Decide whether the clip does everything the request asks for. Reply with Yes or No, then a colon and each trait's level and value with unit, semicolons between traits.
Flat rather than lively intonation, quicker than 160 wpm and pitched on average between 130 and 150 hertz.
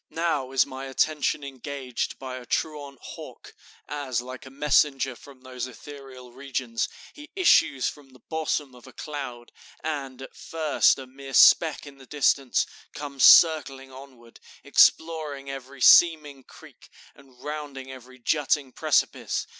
No: narrow, 2.2 semitones; average, 140 wpm; low, 135 Hz